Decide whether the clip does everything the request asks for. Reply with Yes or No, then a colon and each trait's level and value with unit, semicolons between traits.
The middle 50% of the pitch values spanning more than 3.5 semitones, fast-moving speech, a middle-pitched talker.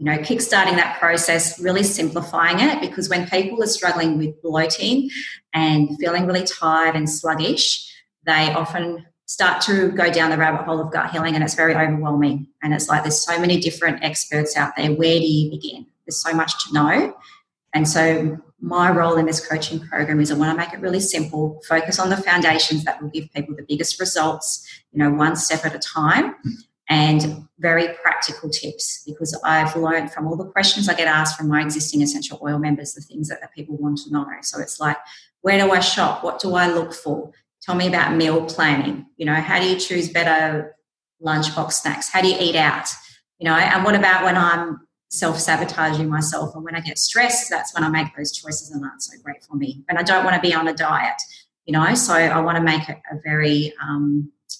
No: narrow, 2.4 semitones; fast, 215 wpm; medium, 160 Hz